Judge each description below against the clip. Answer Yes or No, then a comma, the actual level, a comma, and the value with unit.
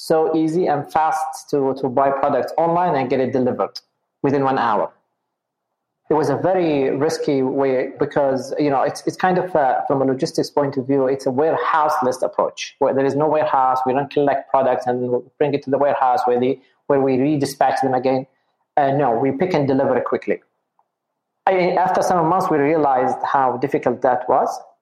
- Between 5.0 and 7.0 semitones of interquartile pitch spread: No, average, 2.8 semitones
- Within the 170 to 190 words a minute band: No, average, 200 wpm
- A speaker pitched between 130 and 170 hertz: Yes, medium, 140 Hz